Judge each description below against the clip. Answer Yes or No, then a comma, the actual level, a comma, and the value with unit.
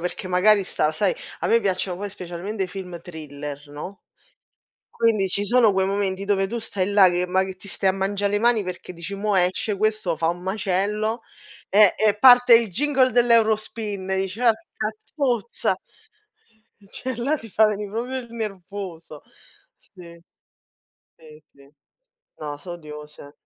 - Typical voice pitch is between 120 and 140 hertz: No, high, 200 Hz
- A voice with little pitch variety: No, average, 3.4 semitones